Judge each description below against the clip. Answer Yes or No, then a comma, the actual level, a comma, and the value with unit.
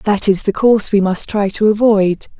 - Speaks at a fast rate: Yes, fast, 225 wpm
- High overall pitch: Yes, high, 205 Hz